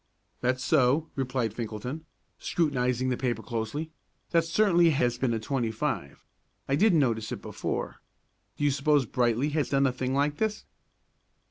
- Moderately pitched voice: No, low, 130 Hz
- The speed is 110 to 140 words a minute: No, average, 150 wpm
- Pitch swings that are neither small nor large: Yes, average, 3.8 semitones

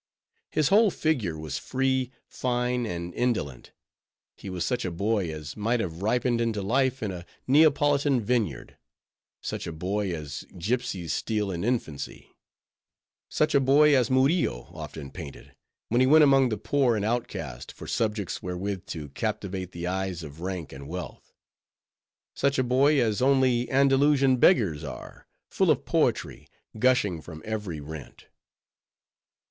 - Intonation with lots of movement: Yes, wide, 6.9 semitones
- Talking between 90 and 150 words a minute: Yes, average, 145 wpm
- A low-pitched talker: Yes, low, 110 Hz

